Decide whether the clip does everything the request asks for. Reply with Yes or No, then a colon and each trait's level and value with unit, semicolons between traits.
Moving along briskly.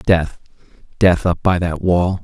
No: average, 160 wpm